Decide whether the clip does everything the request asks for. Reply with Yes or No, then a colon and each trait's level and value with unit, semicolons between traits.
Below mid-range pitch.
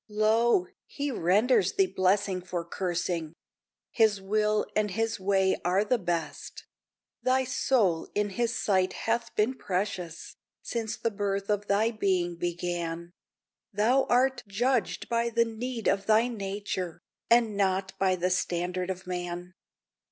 No: high, 200 Hz